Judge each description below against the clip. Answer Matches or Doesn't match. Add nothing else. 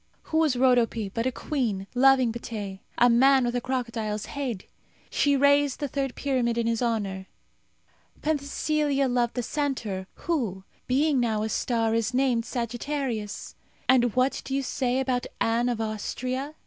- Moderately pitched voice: Doesn't match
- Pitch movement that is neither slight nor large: Matches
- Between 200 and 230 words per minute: Doesn't match